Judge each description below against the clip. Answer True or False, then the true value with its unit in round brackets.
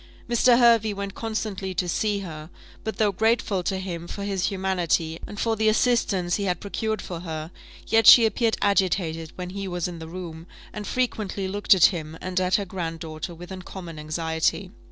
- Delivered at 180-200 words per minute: True (190 wpm)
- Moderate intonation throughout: True (3.4 semitones)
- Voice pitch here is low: False (190 Hz)